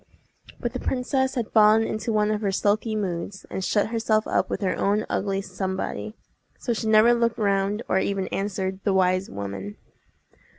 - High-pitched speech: Yes, high, 210 Hz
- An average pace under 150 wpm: No, average, 175 wpm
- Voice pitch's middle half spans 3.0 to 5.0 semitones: No, narrow, 2.5 semitones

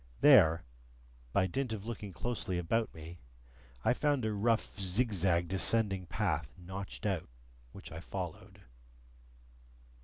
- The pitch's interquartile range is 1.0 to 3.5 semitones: No, average, 4.3 semitones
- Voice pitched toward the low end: Yes, very low, 95 Hz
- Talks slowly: Yes, slow, 120 wpm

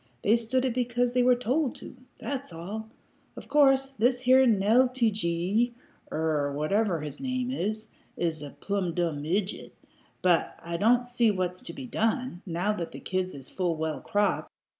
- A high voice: Yes, high, 215 Hz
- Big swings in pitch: Yes, wide, 6.3 semitones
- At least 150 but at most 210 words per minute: Yes, average, 175 wpm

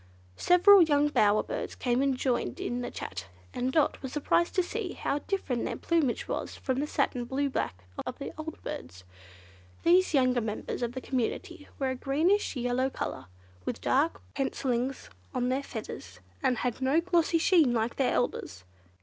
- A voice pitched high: Yes, very high, 265 Hz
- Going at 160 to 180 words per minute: Yes, average, 175 wpm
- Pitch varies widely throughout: No, average, 4.2 semitones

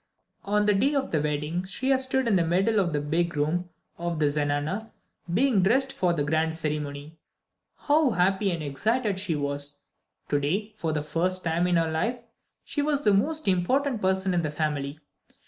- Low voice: No, medium, 175 Hz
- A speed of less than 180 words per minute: No, average, 185 wpm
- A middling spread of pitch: No, wide, 5.8 semitones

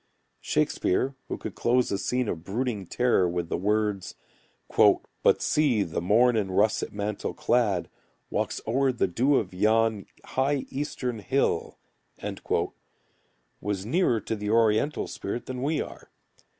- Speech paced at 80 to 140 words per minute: Yes, slow, 135 wpm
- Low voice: Yes, low, 110 Hz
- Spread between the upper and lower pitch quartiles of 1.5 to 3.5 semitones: No, average, 4.2 semitones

